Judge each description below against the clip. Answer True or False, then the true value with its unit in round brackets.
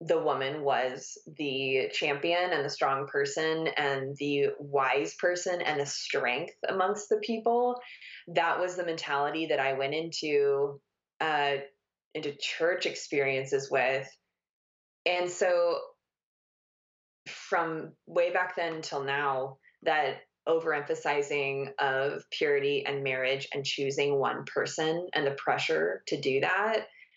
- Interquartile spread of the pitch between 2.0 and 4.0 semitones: False (4.6 semitones)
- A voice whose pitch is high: False (155 Hz)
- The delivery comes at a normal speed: False (125 wpm)